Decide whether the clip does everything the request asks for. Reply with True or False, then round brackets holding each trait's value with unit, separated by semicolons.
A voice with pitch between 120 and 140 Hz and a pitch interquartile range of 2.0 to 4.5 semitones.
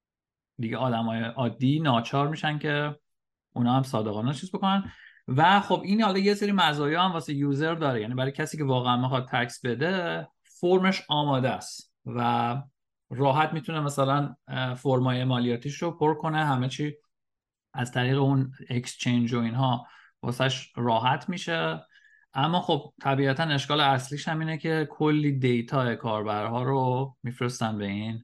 True (135 Hz; 3.8 semitones)